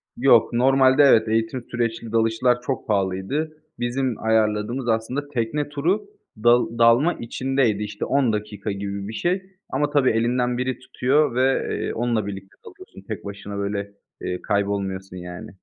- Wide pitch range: No, average, 4.0 semitones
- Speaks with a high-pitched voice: No, low, 115 Hz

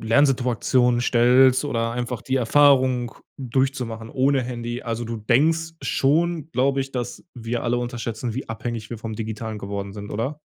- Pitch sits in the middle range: No, low, 120 Hz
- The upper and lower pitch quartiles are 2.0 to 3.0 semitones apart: Yes, narrow, 2.6 semitones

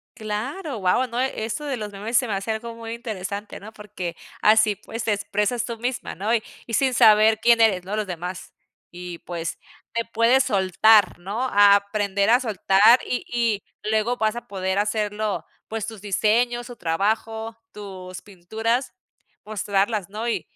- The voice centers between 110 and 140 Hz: No, high, 215 Hz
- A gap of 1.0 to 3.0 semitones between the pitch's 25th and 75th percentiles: Yes, narrow, 2.6 semitones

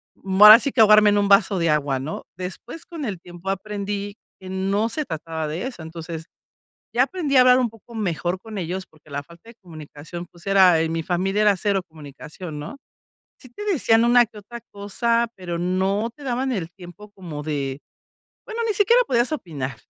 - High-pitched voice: Yes, high, 195 Hz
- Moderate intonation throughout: No, wide, 5.7 semitones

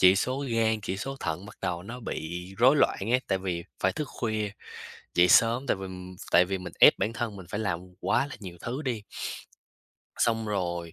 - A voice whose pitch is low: Yes, low, 105 Hz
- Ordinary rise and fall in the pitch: Yes, average, 4.3 semitones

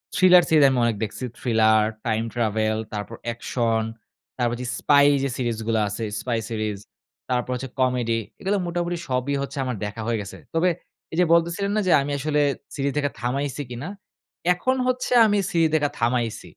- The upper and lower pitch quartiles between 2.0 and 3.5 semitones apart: No, wide, 5.5 semitones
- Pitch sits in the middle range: No, low, 125 Hz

